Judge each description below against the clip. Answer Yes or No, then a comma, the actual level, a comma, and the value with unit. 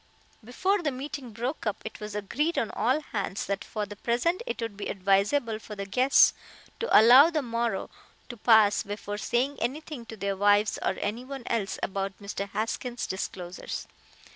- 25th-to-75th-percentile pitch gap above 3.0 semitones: Yes, average, 4.0 semitones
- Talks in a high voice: Yes, high, 225 Hz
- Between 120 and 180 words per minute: Yes, average, 170 wpm